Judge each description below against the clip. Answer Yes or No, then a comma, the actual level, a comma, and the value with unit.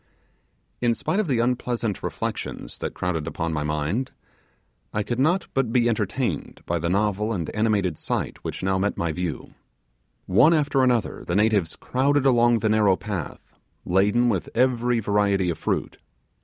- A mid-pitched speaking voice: No, low, 105 Hz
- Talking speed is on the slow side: No, average, 165 wpm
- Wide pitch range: No, average, 4.9 semitones